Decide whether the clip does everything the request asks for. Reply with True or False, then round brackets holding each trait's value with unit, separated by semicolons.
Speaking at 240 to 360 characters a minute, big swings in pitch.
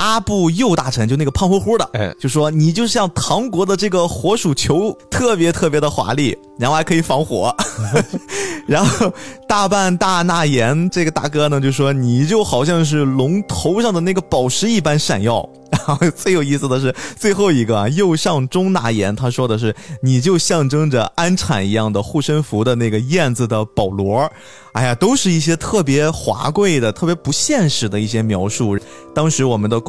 True (275 characters per minute; 6.8 semitones)